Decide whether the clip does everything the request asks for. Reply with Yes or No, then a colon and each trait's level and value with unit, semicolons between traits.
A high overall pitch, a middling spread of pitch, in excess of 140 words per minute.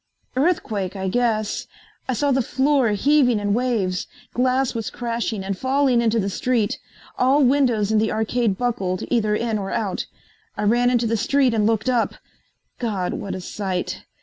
Yes: high, 230 Hz; average, 3.5 semitones; average, 170 wpm